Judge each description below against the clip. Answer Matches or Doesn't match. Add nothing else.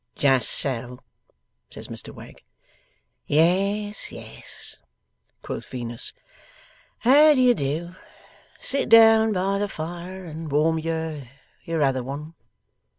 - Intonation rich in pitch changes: Matches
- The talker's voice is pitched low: Doesn't match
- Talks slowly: Matches